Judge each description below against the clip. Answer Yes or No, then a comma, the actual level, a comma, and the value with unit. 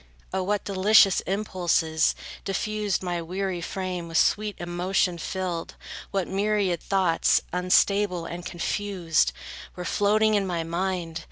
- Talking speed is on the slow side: Yes, slow, 120 wpm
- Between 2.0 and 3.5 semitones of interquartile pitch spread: Yes, narrow, 2.4 semitones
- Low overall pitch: No, medium, 185 Hz